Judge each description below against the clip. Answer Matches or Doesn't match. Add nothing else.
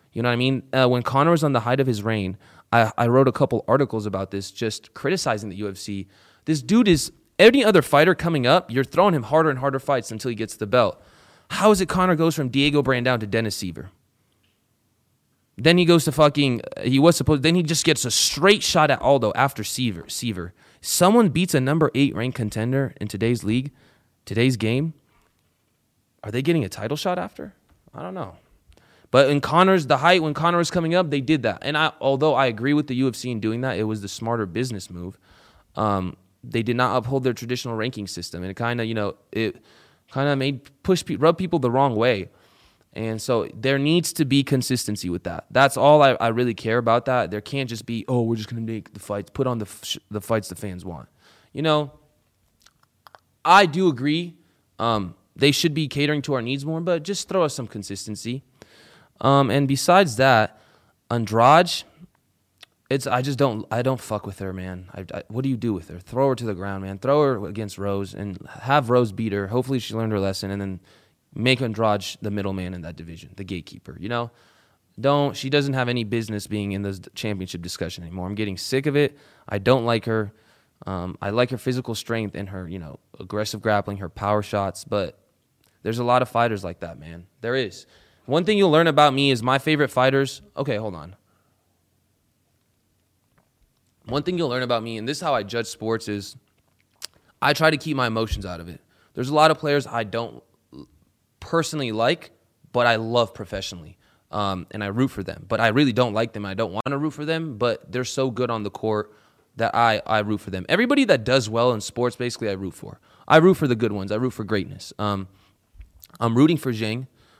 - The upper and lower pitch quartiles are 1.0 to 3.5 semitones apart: Doesn't match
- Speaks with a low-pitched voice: Matches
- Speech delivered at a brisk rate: Matches